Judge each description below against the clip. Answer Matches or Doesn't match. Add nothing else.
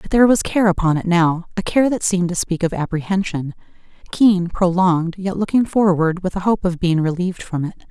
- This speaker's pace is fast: Doesn't match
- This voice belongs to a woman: Matches